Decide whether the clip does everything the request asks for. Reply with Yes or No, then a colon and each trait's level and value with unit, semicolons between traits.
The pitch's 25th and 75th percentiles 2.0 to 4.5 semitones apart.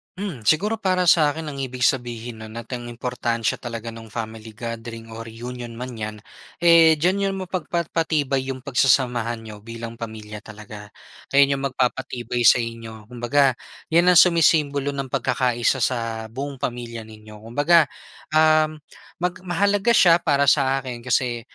No: average, 4.9 semitones